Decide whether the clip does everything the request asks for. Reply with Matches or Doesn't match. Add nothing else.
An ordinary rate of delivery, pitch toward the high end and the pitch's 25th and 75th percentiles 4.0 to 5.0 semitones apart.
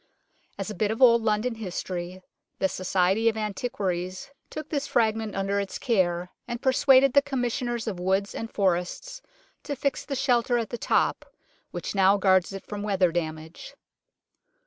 Matches